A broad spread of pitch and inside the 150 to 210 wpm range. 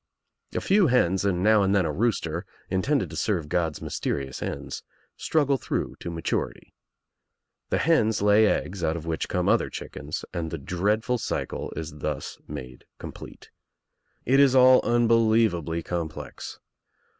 No: wide, 5.9 semitones; average, 140 wpm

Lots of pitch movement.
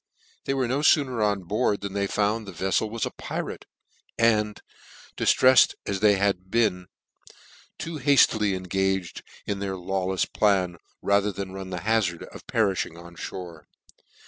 No: average, 2.7 semitones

